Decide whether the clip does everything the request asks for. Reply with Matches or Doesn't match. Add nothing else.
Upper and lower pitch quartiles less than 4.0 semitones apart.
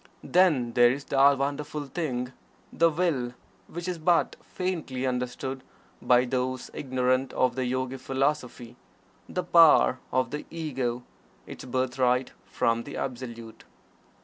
Matches